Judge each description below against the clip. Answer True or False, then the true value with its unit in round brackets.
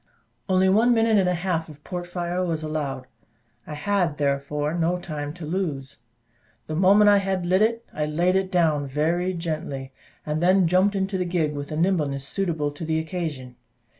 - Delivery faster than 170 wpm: True (185 wpm)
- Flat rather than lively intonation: False (3.7 semitones)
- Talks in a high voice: False (170 Hz)